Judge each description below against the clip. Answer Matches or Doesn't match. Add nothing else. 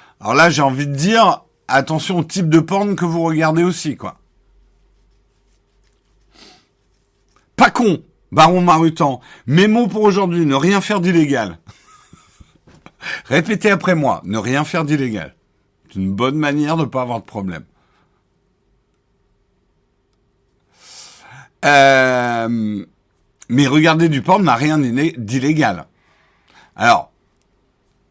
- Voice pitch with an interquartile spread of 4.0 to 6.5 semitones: Matches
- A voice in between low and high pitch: Matches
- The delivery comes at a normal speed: Doesn't match